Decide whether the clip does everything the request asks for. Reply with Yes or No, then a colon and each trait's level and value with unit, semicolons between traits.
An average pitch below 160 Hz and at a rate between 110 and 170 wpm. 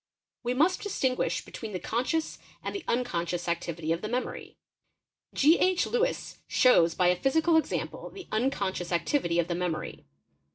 No: high, 230 Hz; average, 155 wpm